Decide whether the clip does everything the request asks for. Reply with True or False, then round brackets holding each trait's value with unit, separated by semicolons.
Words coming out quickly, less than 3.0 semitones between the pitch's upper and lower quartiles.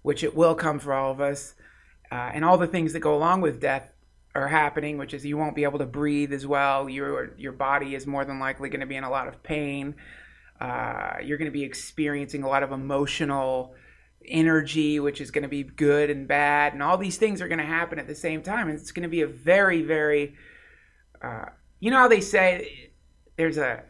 True (230 wpm; 2.5 semitones)